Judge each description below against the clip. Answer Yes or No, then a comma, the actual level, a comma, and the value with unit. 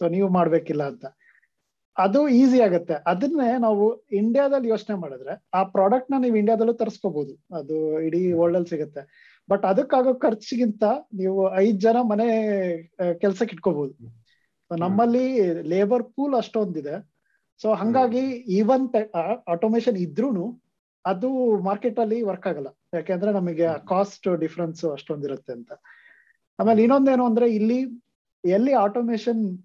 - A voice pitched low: No, high, 205 Hz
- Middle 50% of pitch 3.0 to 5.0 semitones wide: No, wide, 5.6 semitones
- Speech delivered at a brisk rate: Yes, fast, 115 wpm